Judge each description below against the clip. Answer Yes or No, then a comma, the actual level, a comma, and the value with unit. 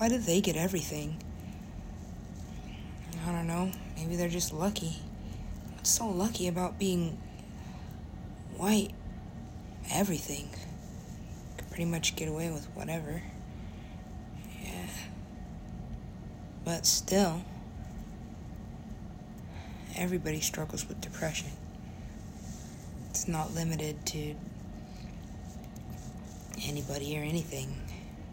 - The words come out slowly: Yes, slow, 85 wpm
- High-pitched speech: No, medium, 140 Hz